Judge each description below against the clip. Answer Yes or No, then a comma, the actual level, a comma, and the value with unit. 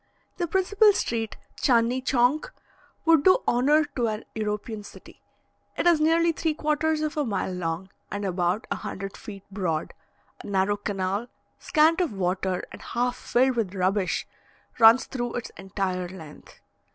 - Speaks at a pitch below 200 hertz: No, high, 225 Hz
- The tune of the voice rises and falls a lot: Yes, wide, 7.8 semitones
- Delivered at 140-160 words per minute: Yes, average, 150 wpm